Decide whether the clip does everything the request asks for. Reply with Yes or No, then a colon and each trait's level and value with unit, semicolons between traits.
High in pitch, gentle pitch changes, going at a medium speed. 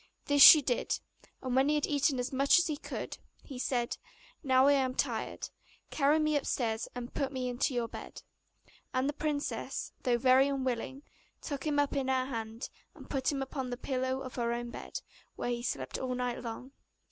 Yes: very high, 260 Hz; narrow, 2.2 semitones; average, 195 wpm